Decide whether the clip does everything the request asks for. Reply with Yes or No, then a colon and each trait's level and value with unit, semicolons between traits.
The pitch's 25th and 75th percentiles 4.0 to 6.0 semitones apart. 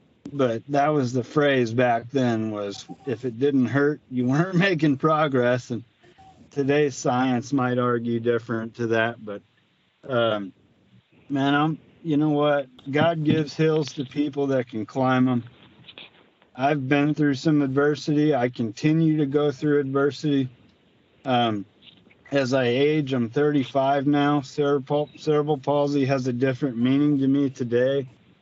No: average, 2.9 semitones